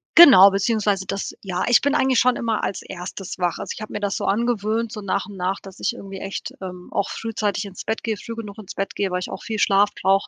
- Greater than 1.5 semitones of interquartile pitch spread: Yes, narrow, 2.6 semitones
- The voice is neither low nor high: No, high, 200 Hz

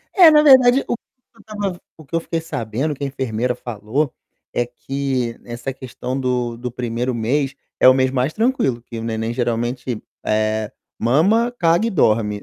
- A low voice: Yes, low, 130 Hz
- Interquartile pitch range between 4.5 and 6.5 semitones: Yes, wide, 5.6 semitones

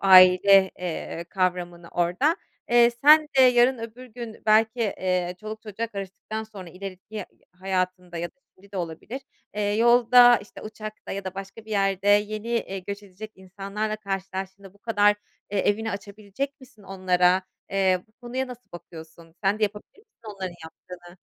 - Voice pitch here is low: No, high, 200 Hz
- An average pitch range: Yes, average, 3.1 semitones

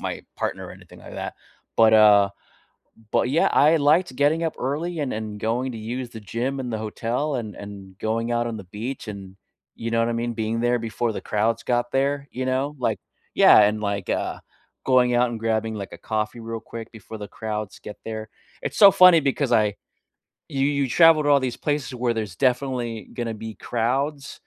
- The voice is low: Yes, low, 115 Hz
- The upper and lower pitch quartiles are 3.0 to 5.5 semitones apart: Yes, average, 3.6 semitones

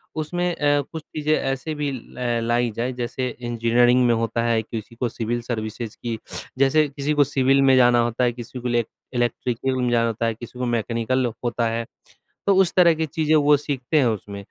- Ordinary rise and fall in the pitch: Yes, average, 3.4 semitones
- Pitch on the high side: No, low, 125 Hz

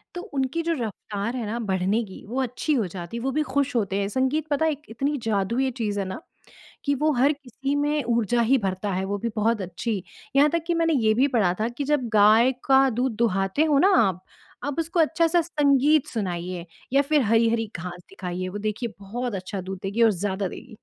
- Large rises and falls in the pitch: Yes, wide, 6.0 semitones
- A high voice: Yes, high, 235 Hz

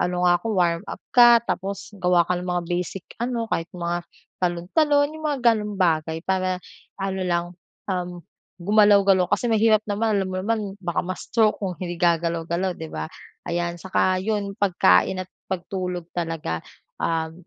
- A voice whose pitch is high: No, medium, 180 Hz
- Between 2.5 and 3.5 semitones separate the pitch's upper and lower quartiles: Yes, average, 2.9 semitones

